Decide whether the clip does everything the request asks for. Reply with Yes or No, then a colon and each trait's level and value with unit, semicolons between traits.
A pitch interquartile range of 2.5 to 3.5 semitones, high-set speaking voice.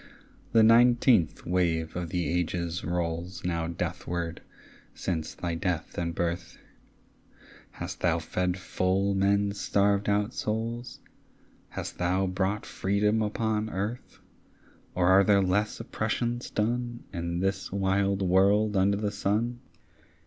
No: average, 3.1 semitones; very low, 95 Hz